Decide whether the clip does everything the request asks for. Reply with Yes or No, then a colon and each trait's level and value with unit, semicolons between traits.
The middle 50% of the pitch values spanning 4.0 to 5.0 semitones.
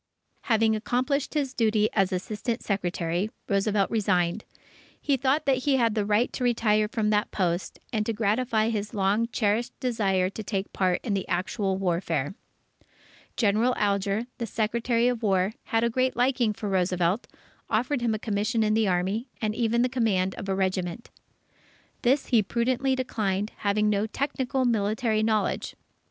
No: average, 3.3 semitones